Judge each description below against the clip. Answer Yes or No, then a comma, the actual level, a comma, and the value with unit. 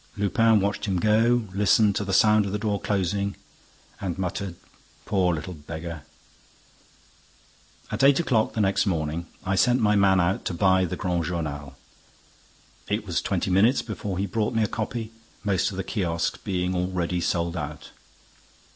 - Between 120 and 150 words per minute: No, average, 165 wpm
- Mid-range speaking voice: No, very low, 95 Hz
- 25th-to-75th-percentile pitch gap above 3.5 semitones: No, average, 3.1 semitones